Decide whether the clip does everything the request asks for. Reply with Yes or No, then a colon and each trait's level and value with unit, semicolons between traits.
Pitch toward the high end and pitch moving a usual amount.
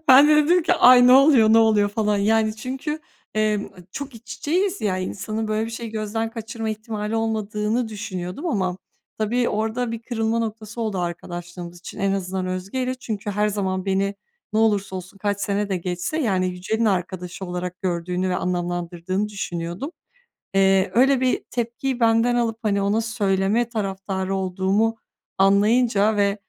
Yes: high, 210 Hz; average, 3.2 semitones